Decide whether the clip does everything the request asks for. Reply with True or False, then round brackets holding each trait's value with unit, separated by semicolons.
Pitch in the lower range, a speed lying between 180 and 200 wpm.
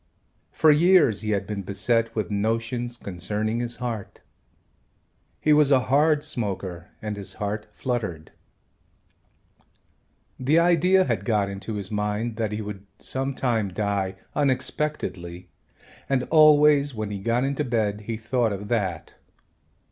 False (115 Hz; 135 wpm)